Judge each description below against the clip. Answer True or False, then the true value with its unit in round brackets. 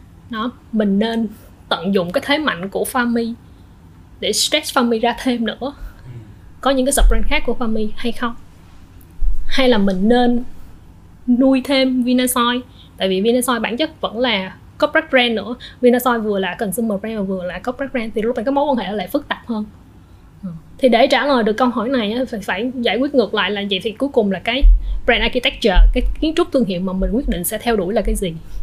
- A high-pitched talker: True (235 Hz)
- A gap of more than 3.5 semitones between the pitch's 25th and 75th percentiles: True (4.2 semitones)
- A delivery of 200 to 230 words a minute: True (210 wpm)